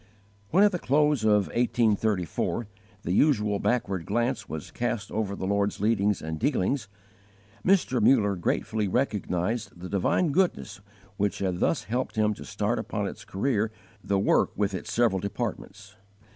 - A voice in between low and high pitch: No, low, 105 Hz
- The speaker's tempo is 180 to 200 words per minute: No, average, 150 wpm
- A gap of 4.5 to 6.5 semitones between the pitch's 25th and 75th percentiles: No, average, 3.8 semitones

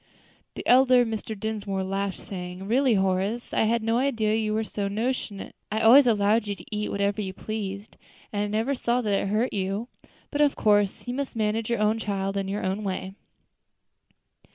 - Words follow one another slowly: No, average, 190 wpm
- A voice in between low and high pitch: No, high, 215 Hz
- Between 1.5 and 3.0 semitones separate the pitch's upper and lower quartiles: Yes, narrow, 2.5 semitones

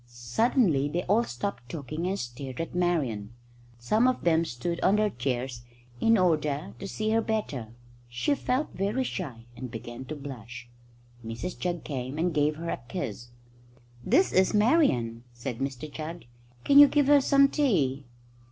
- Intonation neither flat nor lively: No, wide, 8.9 semitones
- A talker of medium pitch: Yes, medium, 155 Hz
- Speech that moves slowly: No, average, 160 wpm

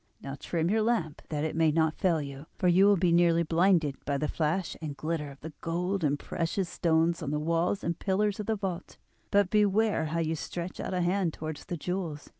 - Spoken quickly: Yes, fast, 225 wpm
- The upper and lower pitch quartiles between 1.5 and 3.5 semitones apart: Yes, average, 3.2 semitones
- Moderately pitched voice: Yes, medium, 170 Hz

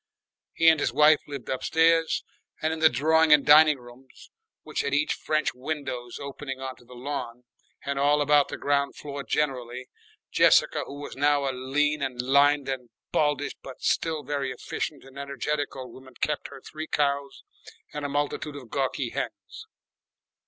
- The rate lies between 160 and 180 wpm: Yes, average, 165 wpm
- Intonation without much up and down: Yes, narrow, 2.1 semitones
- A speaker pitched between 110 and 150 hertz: Yes, medium, 140 Hz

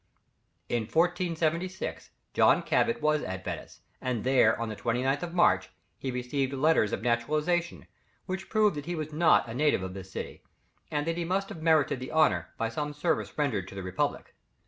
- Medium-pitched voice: Yes, medium, 150 Hz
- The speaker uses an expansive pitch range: Yes, wide, 6.1 semitones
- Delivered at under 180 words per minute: No, average, 185 wpm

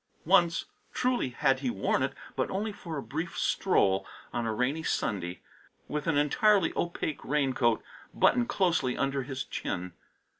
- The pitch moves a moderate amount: No, wide, 5.7 semitones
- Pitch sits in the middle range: Yes, medium, 145 Hz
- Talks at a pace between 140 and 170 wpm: Yes, average, 150 wpm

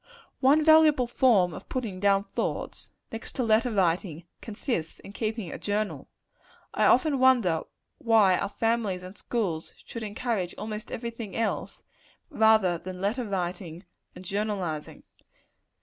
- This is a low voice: No, high, 210 Hz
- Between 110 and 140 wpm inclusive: Yes, slow, 135 wpm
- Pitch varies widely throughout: No, average, 4.1 semitones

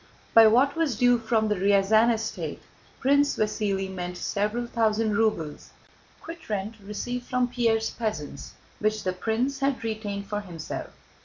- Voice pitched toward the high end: Yes, high, 220 Hz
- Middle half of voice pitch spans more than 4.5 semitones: No, average, 3.1 semitones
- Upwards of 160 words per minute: No, average, 140 wpm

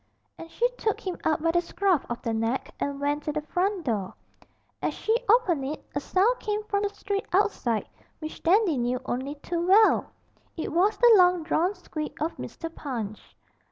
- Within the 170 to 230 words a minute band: Yes, average, 190 wpm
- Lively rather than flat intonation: Yes, wide, 5.9 semitones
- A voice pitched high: Yes, very high, 335 Hz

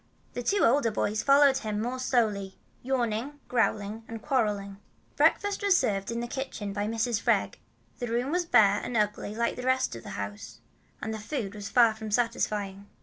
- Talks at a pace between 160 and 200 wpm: Yes, average, 185 wpm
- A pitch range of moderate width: Yes, average, 3.6 semitones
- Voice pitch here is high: Yes, high, 225 Hz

